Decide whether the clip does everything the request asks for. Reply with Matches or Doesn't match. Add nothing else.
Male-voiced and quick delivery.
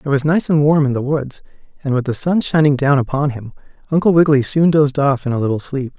Matches